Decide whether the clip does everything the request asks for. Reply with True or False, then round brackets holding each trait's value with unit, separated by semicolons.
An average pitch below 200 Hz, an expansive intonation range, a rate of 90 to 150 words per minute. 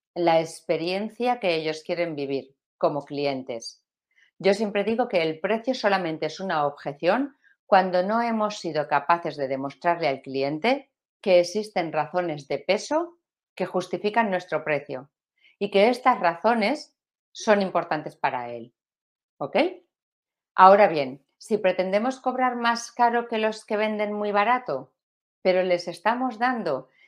True (185 Hz; 6.4 semitones; 135 wpm)